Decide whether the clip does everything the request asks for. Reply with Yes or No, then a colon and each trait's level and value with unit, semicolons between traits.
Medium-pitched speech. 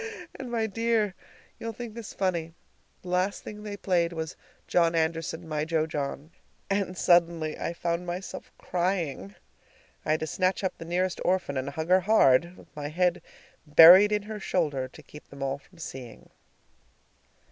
Yes: medium, 170 Hz